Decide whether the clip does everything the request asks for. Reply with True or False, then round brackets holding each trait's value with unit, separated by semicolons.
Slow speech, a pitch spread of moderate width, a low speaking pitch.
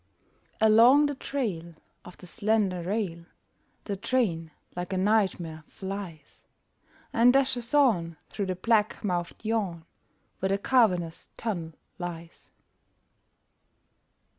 False (110 wpm; 4.8 semitones; 195 Hz)